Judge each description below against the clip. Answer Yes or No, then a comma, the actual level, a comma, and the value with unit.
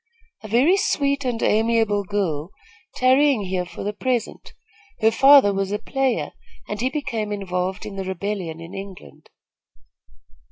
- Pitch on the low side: No, high, 210 Hz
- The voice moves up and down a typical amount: Yes, average, 4.9 semitones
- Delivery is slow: No, average, 145 wpm